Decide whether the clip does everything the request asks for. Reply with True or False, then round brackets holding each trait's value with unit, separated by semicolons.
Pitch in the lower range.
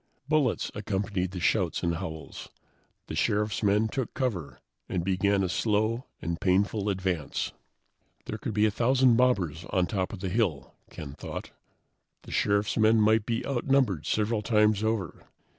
True (105 Hz)